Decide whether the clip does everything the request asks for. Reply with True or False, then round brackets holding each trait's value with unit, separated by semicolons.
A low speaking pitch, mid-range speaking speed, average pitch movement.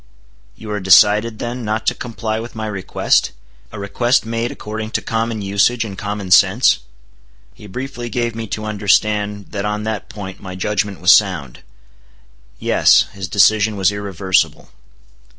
False (105 Hz; 150 wpm; 2.2 semitones)